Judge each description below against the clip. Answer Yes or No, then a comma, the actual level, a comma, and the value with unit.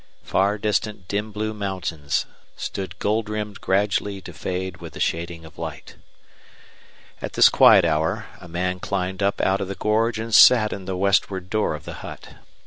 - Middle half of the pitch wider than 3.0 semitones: No, average, 2.7 semitones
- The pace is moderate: Yes, average, 175 wpm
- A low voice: Yes, low, 100 Hz